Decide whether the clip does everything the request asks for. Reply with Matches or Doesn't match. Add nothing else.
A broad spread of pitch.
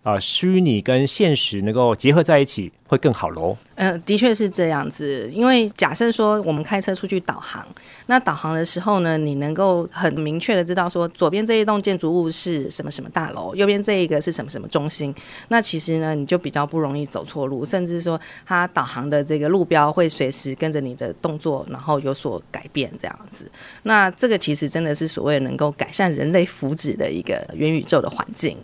Doesn't match